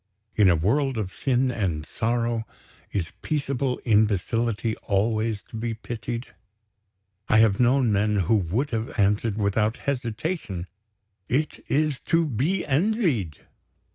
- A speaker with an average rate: No, slow, 125 wpm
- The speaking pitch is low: Yes, low, 115 Hz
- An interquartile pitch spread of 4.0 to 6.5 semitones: Yes, average, 4.3 semitones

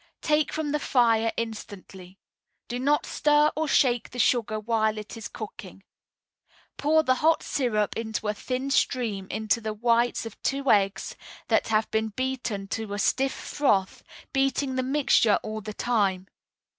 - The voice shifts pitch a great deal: No, average, 3.9 semitones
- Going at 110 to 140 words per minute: No, average, 155 wpm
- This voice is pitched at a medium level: No, high, 230 Hz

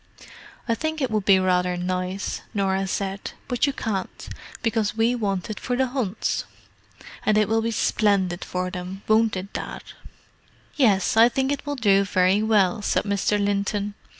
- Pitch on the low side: No, high, 205 Hz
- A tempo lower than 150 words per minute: No, average, 170 wpm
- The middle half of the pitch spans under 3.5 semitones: Yes, average, 3.0 semitones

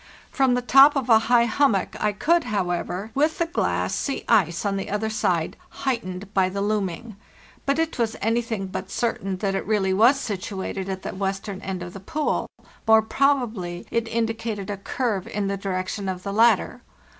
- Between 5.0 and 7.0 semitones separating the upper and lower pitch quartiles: No, average, 3.7 semitones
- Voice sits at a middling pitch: No, high, 210 Hz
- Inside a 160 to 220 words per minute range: Yes, average, 185 wpm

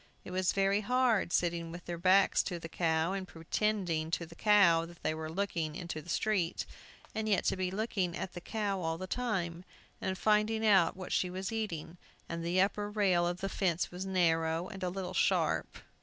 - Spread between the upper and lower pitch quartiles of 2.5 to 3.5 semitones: Yes, average, 3.0 semitones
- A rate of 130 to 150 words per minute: No, average, 200 wpm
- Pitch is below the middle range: No, medium, 185 Hz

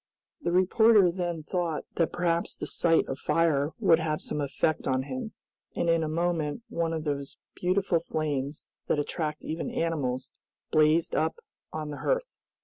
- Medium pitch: Yes, medium, 160 Hz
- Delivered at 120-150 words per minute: No, average, 160 wpm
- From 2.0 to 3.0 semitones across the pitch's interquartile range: Yes, narrow, 2.4 semitones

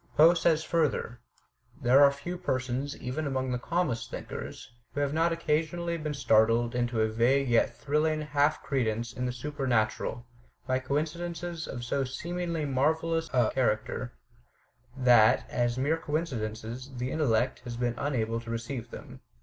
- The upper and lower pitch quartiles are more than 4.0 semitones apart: Yes, average, 4.4 semitones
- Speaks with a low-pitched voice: Yes, low, 130 Hz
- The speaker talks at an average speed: Yes, average, 155 wpm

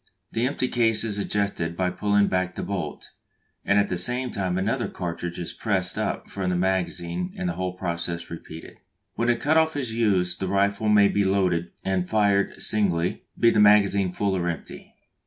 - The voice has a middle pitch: No, low, 100 Hz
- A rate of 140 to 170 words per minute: No, average, 190 wpm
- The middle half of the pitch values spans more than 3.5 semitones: No, average, 3.2 semitones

